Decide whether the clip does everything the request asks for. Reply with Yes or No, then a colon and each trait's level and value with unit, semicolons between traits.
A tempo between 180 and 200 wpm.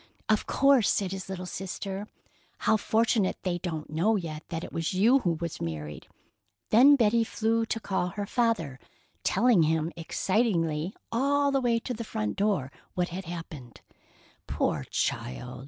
No: average, 155 wpm